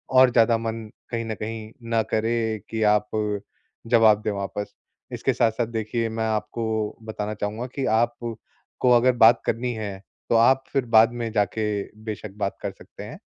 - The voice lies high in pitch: No, low, 110 Hz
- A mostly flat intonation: Yes, narrow, 1.5 semitones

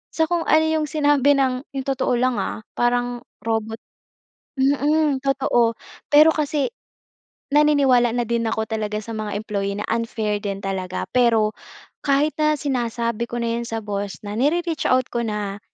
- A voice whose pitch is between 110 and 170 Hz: No, high, 240 Hz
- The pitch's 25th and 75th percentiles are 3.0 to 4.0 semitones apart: No, average, 4.5 semitones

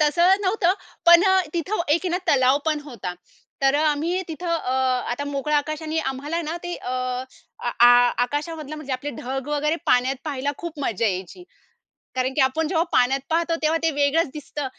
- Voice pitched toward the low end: No, very high, 300 Hz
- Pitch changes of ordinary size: Yes, average, 3.6 semitones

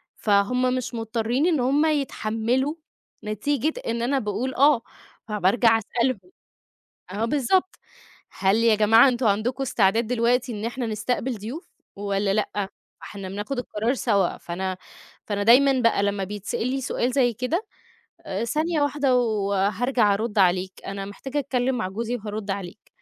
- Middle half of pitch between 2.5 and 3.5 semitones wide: No, average, 4.0 semitones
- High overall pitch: Yes, high, 230 Hz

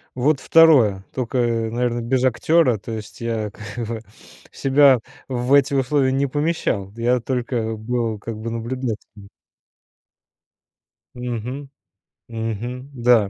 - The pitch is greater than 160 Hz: No, low, 120 Hz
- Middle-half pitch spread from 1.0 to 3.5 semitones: Yes, average, 2.7 semitones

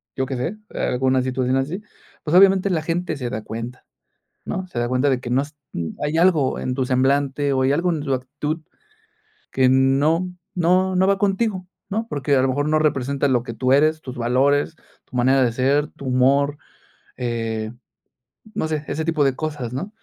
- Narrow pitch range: No, average, 3.7 semitones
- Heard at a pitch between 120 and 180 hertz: Yes, medium, 140 Hz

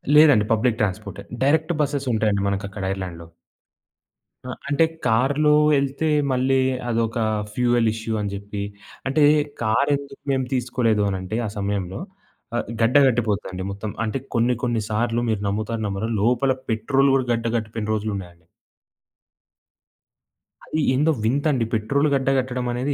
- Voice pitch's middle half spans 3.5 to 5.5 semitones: Yes, average, 4.2 semitones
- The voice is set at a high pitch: No, low, 115 Hz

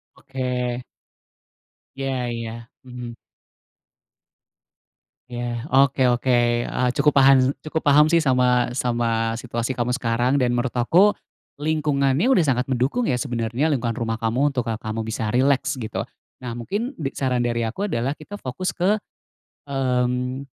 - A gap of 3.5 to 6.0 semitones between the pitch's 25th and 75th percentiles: No, average, 2.8 semitones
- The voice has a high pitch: No, low, 125 Hz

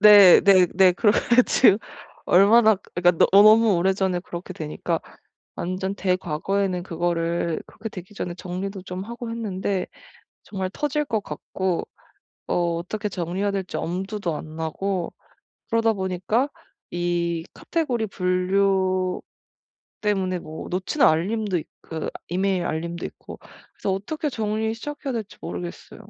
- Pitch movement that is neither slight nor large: Yes, average, 3.1 semitones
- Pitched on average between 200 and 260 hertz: No, high, 190 Hz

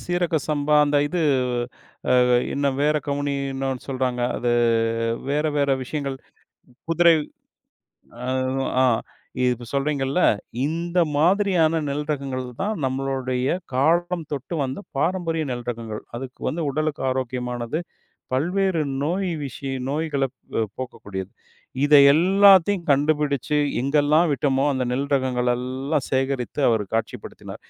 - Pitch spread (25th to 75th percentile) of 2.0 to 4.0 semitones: Yes, average, 3.7 semitones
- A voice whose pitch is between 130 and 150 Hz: Yes, medium, 140 Hz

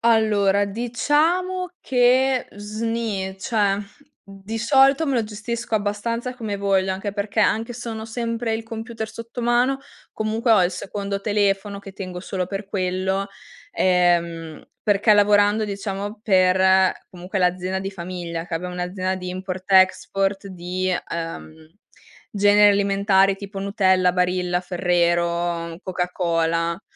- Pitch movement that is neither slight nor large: Yes, average, 3.2 semitones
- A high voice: Yes, high, 195 Hz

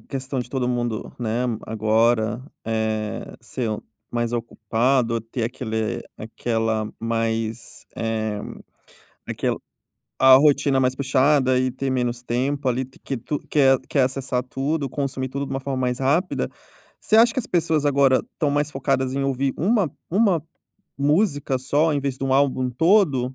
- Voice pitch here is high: No, low, 130 Hz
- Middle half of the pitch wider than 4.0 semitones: No, average, 3.1 semitones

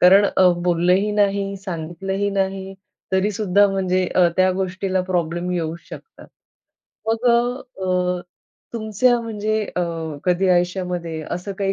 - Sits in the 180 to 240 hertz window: Yes, high, 190 Hz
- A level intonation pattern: Yes, narrow, 1.9 semitones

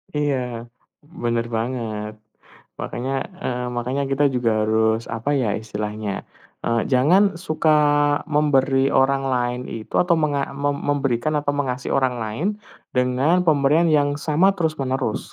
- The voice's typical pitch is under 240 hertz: Yes, low, 135 Hz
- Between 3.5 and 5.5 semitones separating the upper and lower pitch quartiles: Yes, average, 3.8 semitones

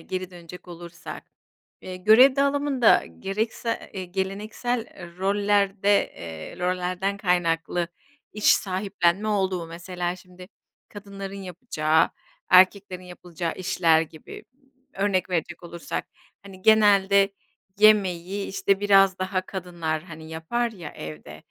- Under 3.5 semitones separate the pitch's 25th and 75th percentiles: Yes, narrow, 2.6 semitones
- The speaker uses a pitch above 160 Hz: Yes, medium, 185 Hz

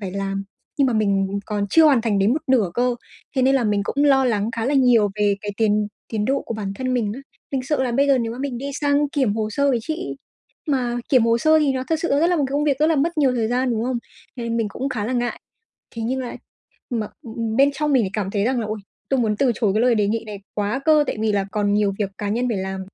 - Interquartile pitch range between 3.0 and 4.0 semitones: No, average, 4.4 semitones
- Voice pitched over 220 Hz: Yes, high, 240 Hz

